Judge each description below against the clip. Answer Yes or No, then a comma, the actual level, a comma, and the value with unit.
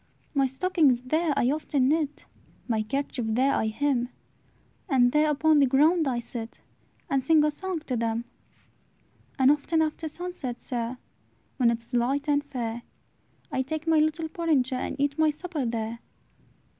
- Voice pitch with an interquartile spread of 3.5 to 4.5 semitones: Yes, average, 4.2 semitones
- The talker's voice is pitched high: Yes, very high, 275 Hz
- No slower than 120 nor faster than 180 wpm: Yes, average, 160 wpm